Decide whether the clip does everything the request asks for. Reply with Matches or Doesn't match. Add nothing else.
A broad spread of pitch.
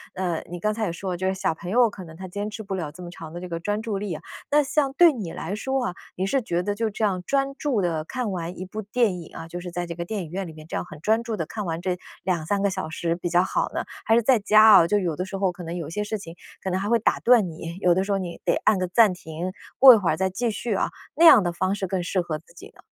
Doesn't match